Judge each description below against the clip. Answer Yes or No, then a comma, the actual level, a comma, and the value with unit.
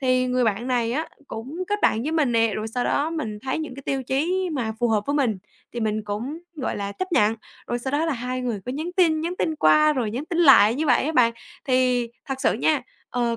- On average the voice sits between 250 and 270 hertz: Yes, very high, 255 Hz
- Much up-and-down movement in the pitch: No, average, 4.8 semitones